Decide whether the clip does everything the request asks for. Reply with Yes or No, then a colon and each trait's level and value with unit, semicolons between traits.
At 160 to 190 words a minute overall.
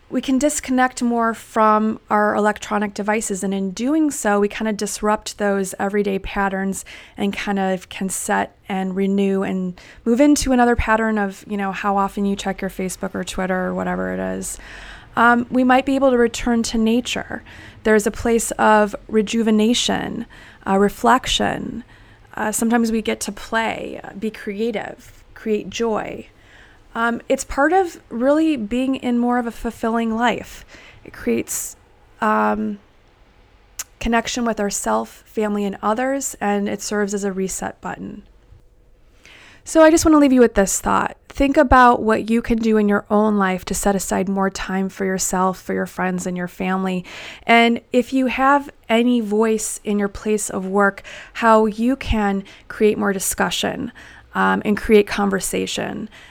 Yes: average, 165 wpm